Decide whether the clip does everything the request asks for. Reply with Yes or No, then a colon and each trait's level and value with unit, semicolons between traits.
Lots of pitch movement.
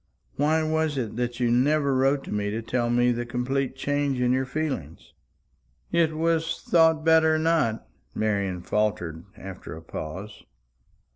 Yes: wide, 6.3 semitones